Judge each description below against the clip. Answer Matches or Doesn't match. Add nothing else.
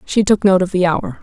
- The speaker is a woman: Matches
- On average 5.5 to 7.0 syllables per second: Doesn't match